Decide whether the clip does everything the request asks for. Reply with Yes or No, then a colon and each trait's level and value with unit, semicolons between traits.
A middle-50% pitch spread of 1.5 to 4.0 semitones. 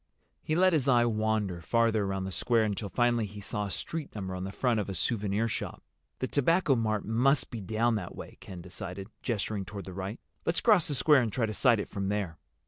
Yes: average, 3.7 semitones